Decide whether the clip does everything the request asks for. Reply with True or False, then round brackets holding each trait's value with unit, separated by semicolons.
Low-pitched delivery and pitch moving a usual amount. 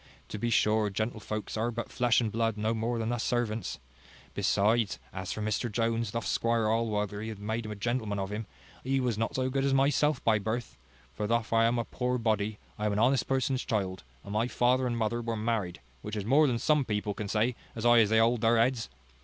False (115 Hz; 2.1 semitones)